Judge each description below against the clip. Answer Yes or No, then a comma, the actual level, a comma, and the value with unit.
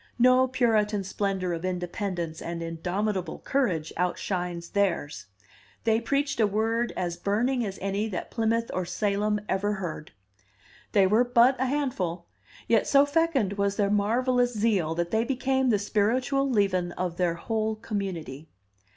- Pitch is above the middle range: Yes, high, 205 Hz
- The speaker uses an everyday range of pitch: Yes, average, 4.7 semitones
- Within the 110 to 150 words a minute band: Yes, average, 145 wpm